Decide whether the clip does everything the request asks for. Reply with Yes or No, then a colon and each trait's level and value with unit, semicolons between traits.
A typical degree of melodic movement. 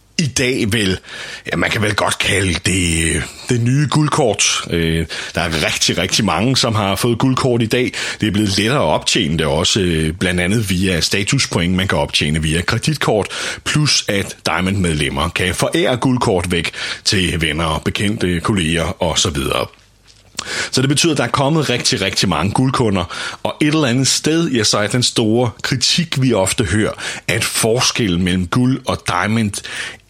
No: wide, 6.1 semitones